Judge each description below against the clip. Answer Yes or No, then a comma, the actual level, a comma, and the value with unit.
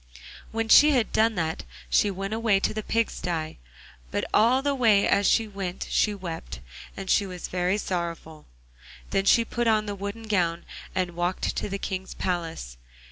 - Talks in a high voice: Yes, high, 195 Hz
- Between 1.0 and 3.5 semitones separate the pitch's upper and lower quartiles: No, average, 3.9 semitones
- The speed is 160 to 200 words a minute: Yes, average, 175 wpm